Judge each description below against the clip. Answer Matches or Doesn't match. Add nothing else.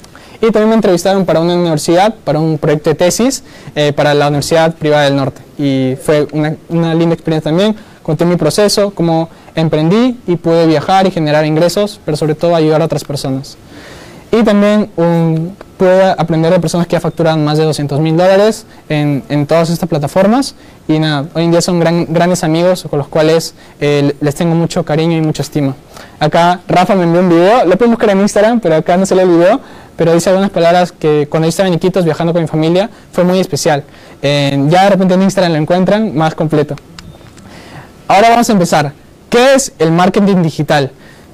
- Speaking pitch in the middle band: Matches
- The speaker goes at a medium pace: Doesn't match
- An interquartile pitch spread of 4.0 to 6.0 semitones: Doesn't match